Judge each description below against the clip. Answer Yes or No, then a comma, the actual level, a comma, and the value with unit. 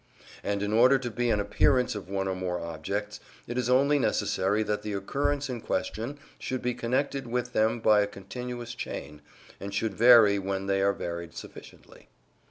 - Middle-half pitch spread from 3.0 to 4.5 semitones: Yes, average, 4.0 semitones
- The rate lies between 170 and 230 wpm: Yes, average, 180 wpm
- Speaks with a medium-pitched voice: No, low, 110 Hz